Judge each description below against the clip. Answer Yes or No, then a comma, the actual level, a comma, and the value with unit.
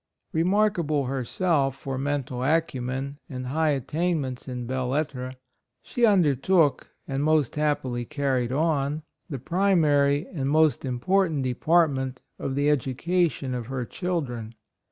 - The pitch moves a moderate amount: Yes, average, 3.6 semitones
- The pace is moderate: No, slow, 130 wpm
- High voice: No, medium, 140 Hz